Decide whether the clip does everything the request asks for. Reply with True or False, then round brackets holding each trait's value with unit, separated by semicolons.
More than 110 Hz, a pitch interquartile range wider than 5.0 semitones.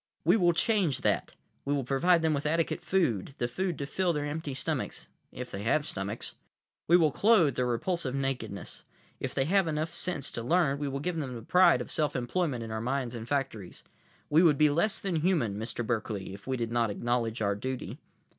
True (140 Hz; 5.6 semitones)